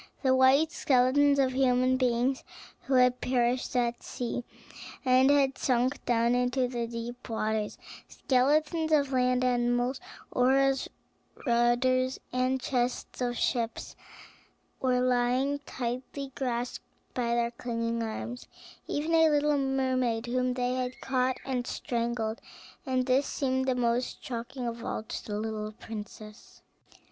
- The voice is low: No, very high, 250 Hz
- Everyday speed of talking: No, slow, 130 wpm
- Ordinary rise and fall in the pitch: No, narrow, 1.6 semitones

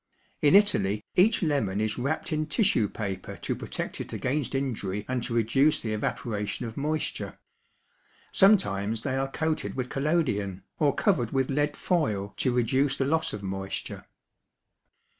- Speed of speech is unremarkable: Yes, average, 150 wpm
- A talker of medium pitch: No, low, 130 Hz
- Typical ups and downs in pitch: No, wide, 6.4 semitones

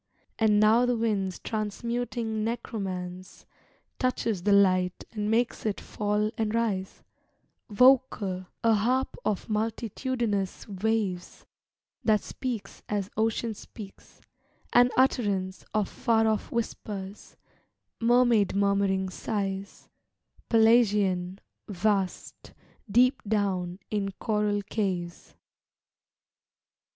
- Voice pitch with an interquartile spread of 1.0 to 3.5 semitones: Yes, average, 2.8 semitones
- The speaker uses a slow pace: Yes, slow, 95 wpm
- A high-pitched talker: Yes, high, 210 Hz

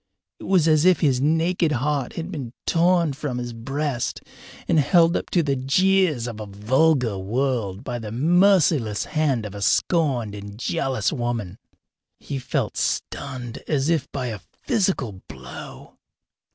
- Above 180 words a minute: No, average, 150 wpm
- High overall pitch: No, low, 135 Hz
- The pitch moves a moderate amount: No, wide, 5.7 semitones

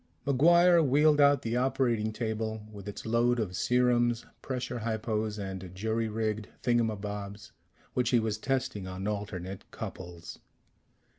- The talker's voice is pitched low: Yes, low, 110 Hz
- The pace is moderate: No, slow, 130 wpm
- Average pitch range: Yes, average, 3.1 semitones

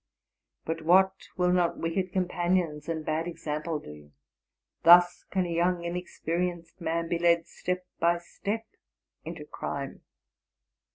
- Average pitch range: No, narrow, 1.6 semitones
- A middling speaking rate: No, slow, 125 wpm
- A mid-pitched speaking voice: Yes, medium, 170 Hz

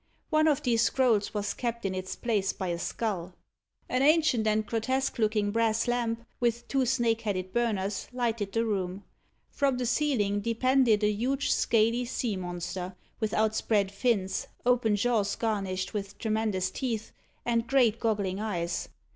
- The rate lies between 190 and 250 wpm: No, average, 155 wpm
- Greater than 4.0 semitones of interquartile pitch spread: No, average, 3.1 semitones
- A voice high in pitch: Yes, high, 220 Hz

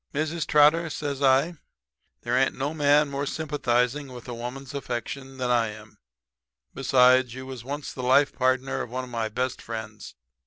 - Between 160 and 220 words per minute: Yes, average, 165 wpm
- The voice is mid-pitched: No, low, 130 Hz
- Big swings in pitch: No, narrow, 2.6 semitones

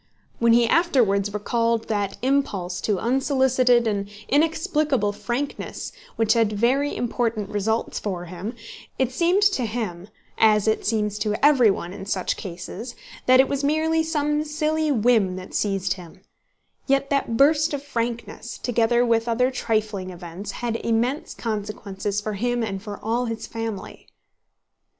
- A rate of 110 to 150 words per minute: Yes, average, 140 wpm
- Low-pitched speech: No, high, 230 Hz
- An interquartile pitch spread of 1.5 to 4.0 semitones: No, average, 4.4 semitones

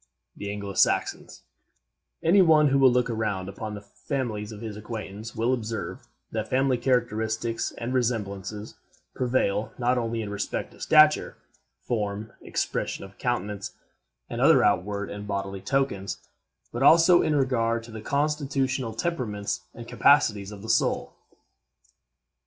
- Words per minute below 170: Yes, average, 140 wpm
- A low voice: Yes, low, 115 Hz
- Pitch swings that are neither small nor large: Yes, average, 3.9 semitones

